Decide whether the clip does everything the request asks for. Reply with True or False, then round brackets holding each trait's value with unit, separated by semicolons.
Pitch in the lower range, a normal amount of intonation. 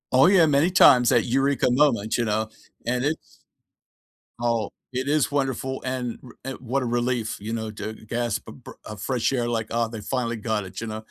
True (120 Hz; 3.1 semitones)